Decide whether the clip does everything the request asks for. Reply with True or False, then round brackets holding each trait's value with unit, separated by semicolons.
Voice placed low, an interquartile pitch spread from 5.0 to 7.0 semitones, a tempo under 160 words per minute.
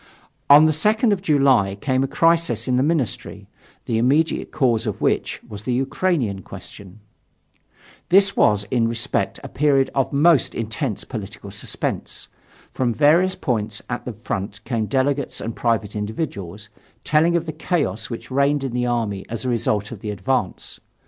False (125 Hz; 5.6 semitones; 165 wpm)